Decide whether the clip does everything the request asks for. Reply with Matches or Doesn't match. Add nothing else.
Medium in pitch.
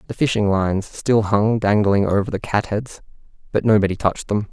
Doesn't match